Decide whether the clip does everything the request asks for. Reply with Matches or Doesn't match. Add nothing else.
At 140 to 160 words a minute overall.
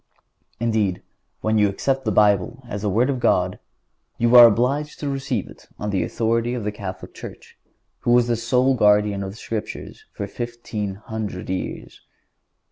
Doesn't match